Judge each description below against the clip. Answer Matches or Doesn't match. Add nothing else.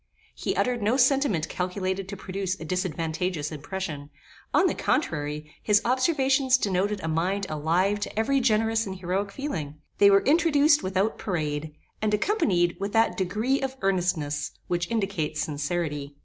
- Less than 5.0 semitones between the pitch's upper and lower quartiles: Doesn't match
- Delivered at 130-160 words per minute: Matches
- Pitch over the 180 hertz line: Matches